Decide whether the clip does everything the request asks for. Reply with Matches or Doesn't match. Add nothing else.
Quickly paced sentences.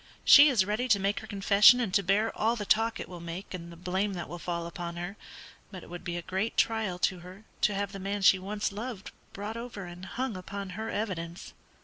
Matches